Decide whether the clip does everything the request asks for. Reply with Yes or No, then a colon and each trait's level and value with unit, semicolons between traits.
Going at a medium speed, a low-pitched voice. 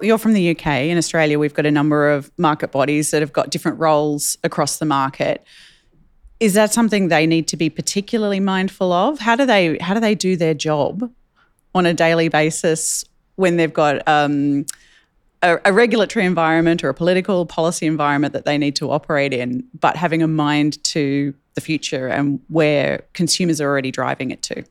No: average, 190 wpm; medium, 160 Hz